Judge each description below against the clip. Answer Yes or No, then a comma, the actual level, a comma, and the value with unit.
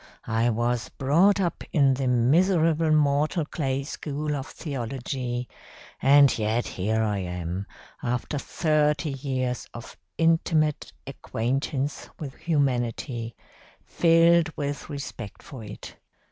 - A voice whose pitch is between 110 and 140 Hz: Yes, low, 135 Hz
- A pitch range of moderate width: Yes, average, 4.2 semitones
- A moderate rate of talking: No, slow, 110 wpm